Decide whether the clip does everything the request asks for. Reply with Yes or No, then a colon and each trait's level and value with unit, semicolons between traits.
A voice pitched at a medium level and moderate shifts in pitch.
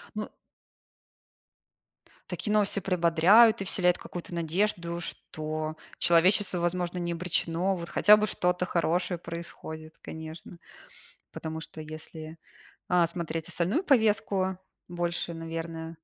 No: medium, 170 Hz; narrow, 2.2 semitones